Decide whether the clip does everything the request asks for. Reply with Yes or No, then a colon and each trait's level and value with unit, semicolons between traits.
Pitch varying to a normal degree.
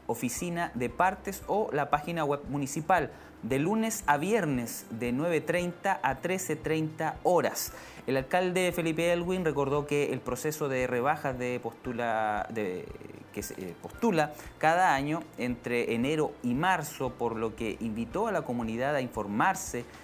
No: wide, 5.8 semitones